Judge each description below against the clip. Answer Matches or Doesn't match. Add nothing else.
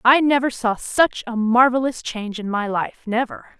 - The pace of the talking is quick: Doesn't match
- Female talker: Matches